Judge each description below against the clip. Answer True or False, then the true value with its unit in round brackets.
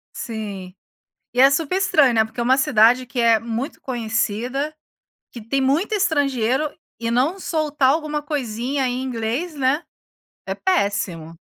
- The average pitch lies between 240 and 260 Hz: True (255 Hz)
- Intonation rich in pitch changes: False (4.4 semitones)